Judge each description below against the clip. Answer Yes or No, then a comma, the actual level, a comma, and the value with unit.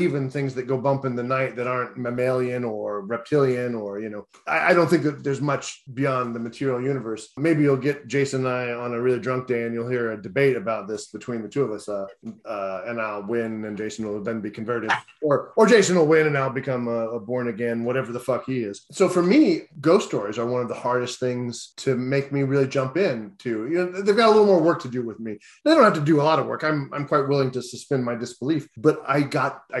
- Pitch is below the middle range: Yes, low, 125 Hz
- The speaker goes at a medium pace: No, fast, 260 wpm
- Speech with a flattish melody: No, average, 3.3 semitones